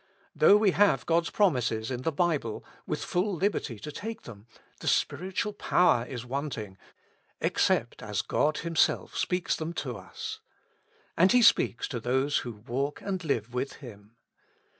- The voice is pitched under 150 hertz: Yes, medium, 140 Hz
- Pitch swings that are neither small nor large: No, wide, 7.0 semitones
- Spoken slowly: No, average, 155 wpm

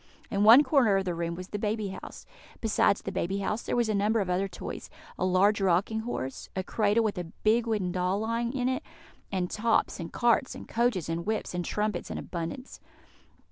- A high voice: Yes, high, 205 Hz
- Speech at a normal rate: No, fast, 210 wpm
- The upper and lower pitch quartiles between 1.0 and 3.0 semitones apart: No, average, 3.5 semitones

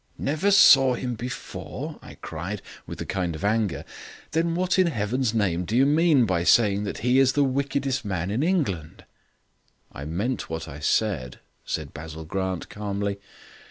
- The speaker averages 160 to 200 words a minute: Yes, average, 165 wpm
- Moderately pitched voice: No, low, 110 Hz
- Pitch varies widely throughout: Yes, wide, 6.9 semitones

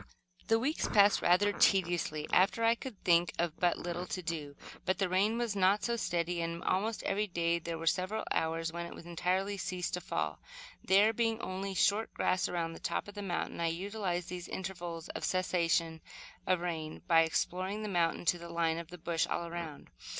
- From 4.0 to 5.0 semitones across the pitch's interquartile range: No, average, 2.8 semitones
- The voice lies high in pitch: No, medium, 180 Hz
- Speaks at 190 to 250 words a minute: Yes, average, 200 wpm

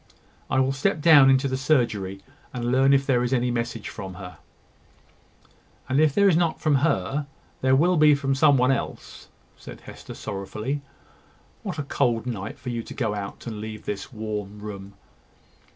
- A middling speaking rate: Yes, average, 180 wpm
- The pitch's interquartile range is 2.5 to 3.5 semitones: No, average, 4.6 semitones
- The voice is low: Yes, low, 125 Hz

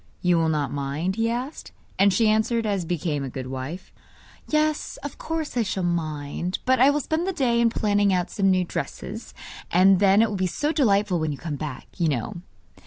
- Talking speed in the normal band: No, fast, 210 wpm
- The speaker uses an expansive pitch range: Yes, wide, 6.3 semitones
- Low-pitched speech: No, high, 190 Hz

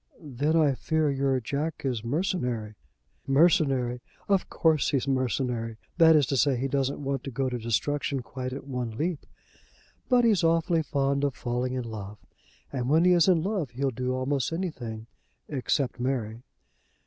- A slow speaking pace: No, average, 165 wpm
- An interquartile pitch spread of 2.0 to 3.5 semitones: No, average, 3.9 semitones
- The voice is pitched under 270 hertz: Yes, low, 135 Hz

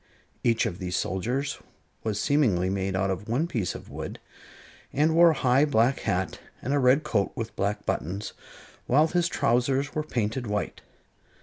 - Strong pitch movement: Yes, wide, 6.1 semitones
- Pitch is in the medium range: No, low, 115 Hz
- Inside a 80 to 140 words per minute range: No, average, 170 wpm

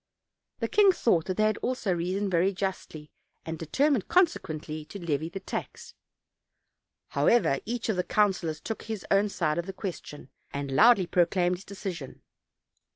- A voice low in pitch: No, medium, 185 Hz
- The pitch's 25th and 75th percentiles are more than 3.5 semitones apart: Yes, average, 4.5 semitones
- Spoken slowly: No, average, 155 wpm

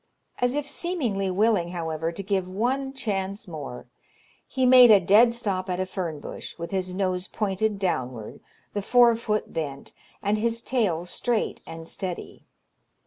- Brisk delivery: No, average, 155 wpm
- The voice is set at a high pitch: Yes, high, 195 Hz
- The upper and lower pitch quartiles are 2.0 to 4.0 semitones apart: No, average, 4.6 semitones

